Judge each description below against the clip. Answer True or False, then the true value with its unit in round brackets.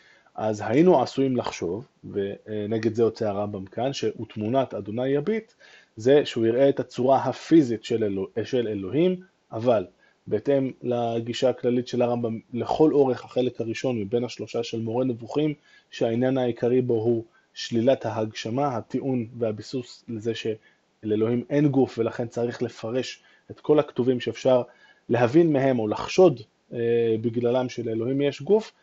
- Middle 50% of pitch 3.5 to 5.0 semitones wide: False (2.9 semitones)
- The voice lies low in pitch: True (120 Hz)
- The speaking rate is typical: True (135 wpm)